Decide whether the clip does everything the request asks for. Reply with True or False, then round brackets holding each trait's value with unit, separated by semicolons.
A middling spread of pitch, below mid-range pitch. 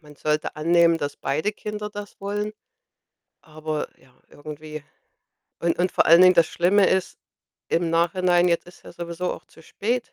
False (3.1 semitones; 170 Hz)